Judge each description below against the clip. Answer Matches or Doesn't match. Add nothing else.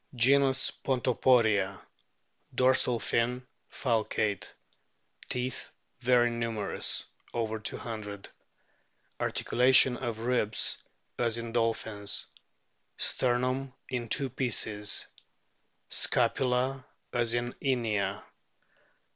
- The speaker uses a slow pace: Matches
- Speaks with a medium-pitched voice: Doesn't match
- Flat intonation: Matches